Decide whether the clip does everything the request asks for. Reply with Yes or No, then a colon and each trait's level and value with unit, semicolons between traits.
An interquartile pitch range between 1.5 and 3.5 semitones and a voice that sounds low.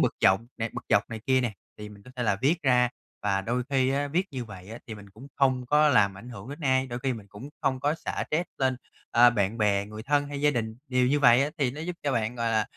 No: average, 4.2 semitones; low, 125 Hz